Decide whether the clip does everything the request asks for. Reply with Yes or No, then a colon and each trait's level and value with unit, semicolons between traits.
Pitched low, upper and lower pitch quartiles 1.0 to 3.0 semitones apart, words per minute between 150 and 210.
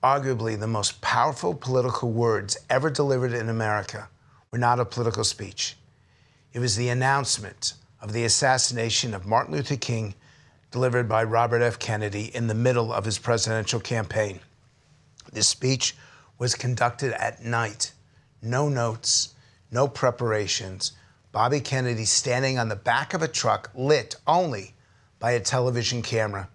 No: low, 120 Hz; average, 2.7 semitones; average, 140 wpm